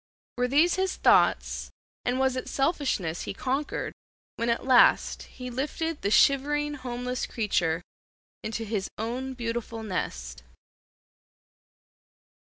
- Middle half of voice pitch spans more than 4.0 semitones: No, average, 3.7 semitones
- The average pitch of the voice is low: No, very high, 250 Hz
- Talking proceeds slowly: Yes, slow, 115 wpm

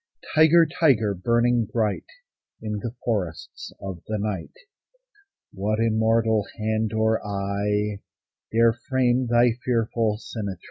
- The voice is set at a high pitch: No, low, 110 Hz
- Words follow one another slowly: Yes, slow, 110 wpm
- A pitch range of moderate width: No, narrow, 2.3 semitones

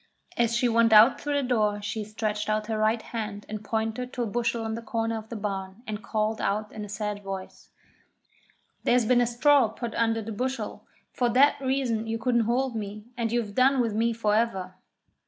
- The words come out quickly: Yes, fast, 210 wpm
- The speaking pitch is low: No, high, 225 Hz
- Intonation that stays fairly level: Yes, narrow, 2.0 semitones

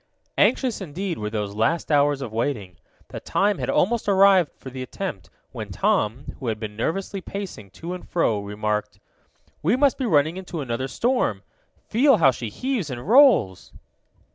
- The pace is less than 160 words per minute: No, average, 165 wpm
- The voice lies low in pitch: No, medium, 145 Hz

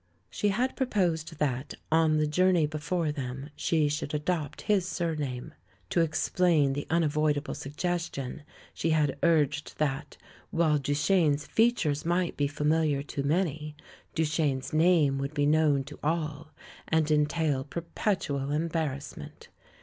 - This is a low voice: No, medium, 155 Hz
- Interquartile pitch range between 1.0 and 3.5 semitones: Yes, narrow, 2.5 semitones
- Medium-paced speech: No, slow, 125 wpm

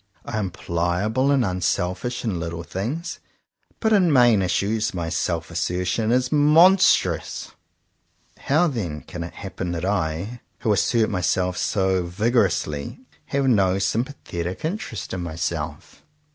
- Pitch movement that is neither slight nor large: No, wide, 5.9 semitones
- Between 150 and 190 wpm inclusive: No, slow, 135 wpm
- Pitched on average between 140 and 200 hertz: No, very low, 95 Hz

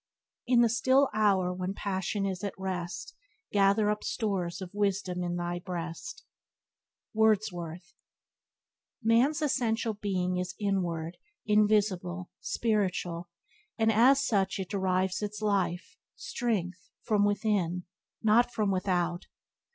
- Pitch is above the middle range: Yes, high, 195 Hz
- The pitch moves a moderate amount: Yes, average, 3.1 semitones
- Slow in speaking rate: Yes, slow, 120 wpm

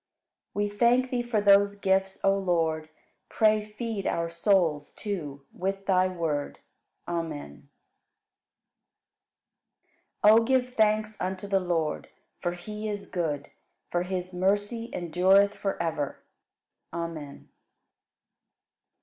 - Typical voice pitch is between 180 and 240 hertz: Yes, high, 190 Hz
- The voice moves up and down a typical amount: Yes, average, 3.8 semitones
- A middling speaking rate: No, slow, 110 wpm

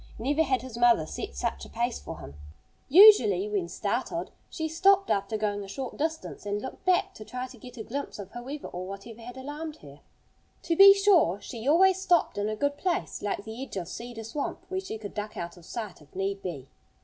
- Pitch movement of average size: No, wide, 7.1 semitones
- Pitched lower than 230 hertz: No, high, 235 Hz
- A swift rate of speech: Yes, fast, 220 wpm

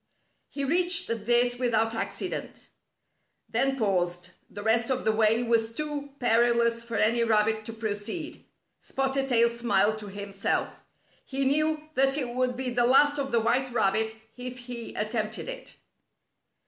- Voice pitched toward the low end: No, high, 235 Hz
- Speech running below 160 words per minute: Yes, average, 150 wpm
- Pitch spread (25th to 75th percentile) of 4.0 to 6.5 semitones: No, average, 3.4 semitones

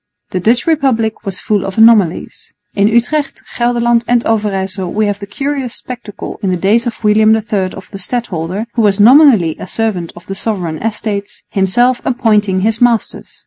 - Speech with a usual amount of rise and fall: Yes, average, 3.5 semitones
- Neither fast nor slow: Yes, average, 175 wpm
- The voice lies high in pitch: Yes, high, 215 Hz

